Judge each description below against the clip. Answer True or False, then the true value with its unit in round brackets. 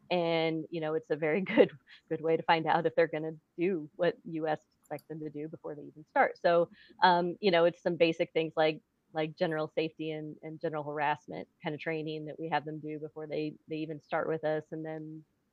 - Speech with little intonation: True (1.3 semitones)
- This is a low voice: False (160 Hz)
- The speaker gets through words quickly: True (230 wpm)